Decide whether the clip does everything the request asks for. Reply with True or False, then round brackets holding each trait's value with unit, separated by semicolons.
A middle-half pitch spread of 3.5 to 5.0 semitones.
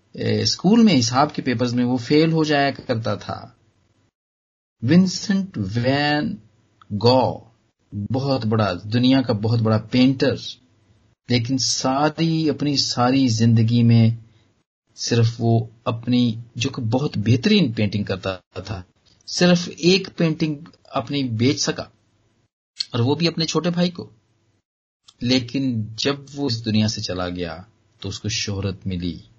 True (4.3 semitones)